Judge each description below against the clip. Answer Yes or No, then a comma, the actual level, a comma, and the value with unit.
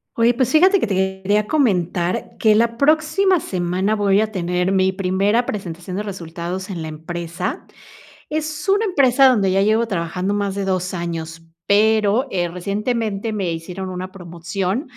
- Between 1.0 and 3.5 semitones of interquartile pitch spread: No, average, 4.2 semitones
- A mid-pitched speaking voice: No, high, 195 Hz